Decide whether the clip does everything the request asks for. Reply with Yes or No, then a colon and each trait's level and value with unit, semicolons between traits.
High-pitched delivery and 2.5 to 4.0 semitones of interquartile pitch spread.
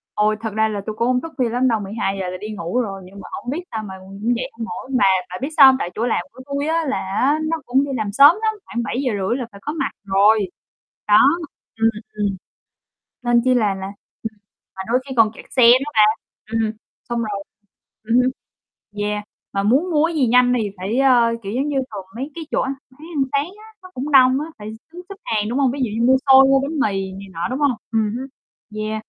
No: high, 235 Hz; average, 4.4 semitones